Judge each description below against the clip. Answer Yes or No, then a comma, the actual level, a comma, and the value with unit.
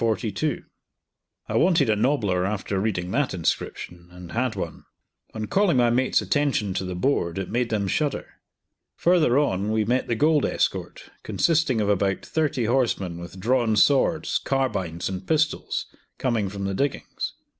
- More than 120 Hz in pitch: No, low, 110 Hz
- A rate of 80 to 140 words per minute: No, average, 155 wpm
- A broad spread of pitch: Yes, wide, 6.4 semitones